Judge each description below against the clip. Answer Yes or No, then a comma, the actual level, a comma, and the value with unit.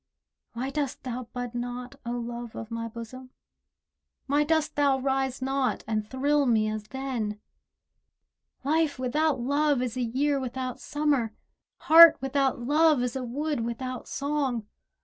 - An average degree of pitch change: Yes, average, 3.0 semitones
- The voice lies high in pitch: Yes, very high, 260 Hz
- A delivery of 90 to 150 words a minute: Yes, average, 145 wpm